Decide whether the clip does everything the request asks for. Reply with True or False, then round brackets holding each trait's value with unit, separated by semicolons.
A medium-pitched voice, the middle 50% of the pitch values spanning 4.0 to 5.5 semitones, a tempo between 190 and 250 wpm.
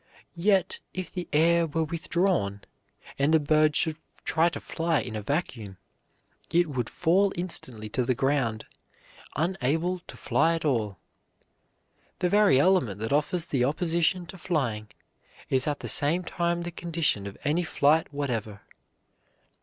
False (155 Hz; 5.1 semitones; 145 wpm)